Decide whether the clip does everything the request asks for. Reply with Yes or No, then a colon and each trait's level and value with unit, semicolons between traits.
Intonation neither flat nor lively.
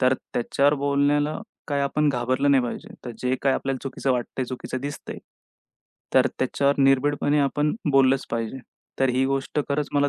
No: narrow, 1.7 semitones